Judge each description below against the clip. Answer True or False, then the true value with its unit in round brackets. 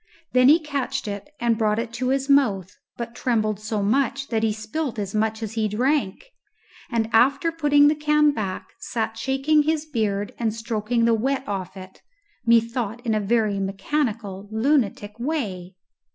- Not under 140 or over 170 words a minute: True (165 wpm)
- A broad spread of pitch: False (4.4 semitones)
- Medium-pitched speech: False (230 Hz)